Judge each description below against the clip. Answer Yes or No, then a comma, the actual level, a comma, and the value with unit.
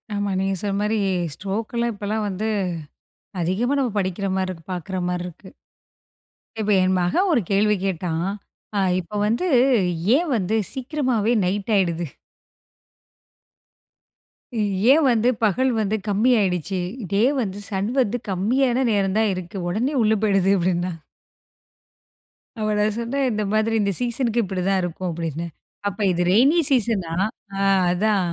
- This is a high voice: Yes, high, 205 Hz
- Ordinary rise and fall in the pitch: Yes, average, 3.6 semitones